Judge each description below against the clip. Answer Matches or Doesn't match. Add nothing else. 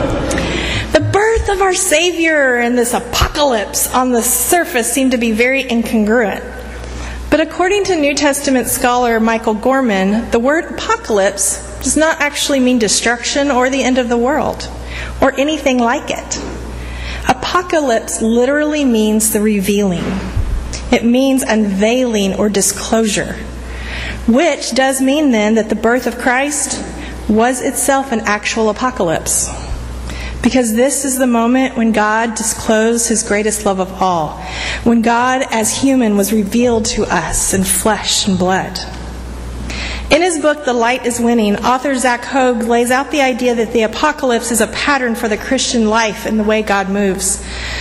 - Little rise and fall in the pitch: Doesn't match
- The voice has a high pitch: Matches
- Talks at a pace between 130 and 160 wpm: Matches